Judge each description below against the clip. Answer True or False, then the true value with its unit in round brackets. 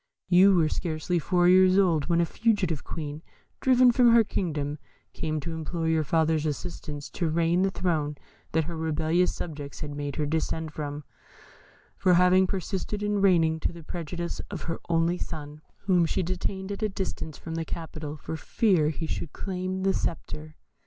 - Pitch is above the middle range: False (165 Hz)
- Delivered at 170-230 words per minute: True (175 wpm)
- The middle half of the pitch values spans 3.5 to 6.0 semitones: False (3.0 semitones)